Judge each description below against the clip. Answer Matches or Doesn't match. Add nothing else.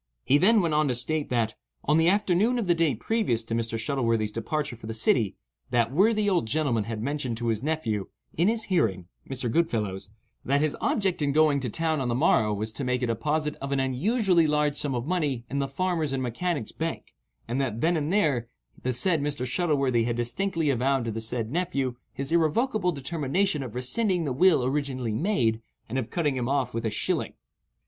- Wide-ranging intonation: Matches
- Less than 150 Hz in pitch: Matches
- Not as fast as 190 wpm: Doesn't match